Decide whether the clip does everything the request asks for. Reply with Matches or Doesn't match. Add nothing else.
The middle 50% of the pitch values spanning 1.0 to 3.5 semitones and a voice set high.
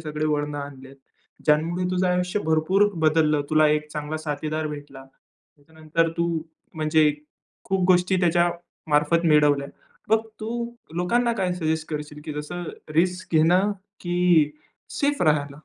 Doesn't match